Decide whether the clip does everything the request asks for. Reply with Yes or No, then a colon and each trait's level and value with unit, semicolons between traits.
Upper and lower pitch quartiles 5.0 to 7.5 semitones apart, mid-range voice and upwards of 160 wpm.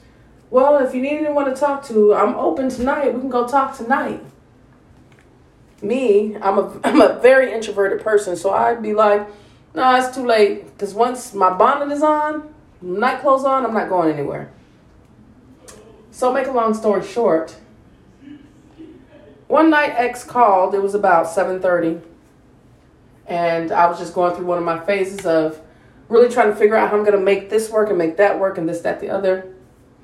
No: wide, 5.4 semitones; high, 215 Hz; average, 185 wpm